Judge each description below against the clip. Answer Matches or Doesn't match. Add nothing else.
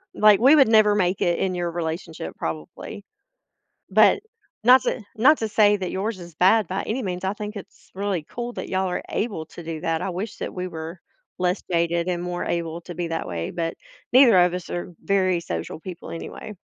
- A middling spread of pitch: Matches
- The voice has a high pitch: Doesn't match